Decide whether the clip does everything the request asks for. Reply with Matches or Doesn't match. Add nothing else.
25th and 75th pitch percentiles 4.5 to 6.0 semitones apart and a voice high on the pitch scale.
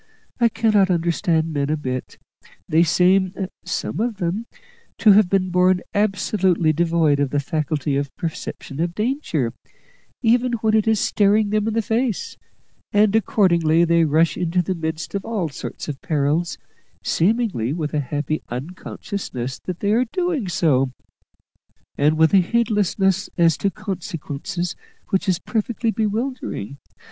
Doesn't match